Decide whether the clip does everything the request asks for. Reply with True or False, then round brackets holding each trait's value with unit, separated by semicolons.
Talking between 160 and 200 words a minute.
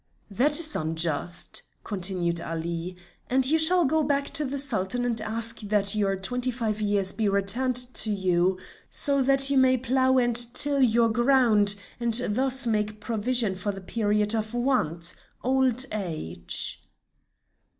False (150 wpm)